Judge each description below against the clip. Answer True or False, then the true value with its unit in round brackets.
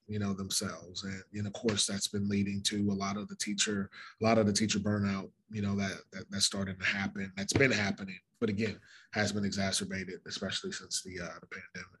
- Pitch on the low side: True (100 Hz)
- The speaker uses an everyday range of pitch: False (1.1 semitones)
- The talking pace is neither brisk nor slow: False (220 wpm)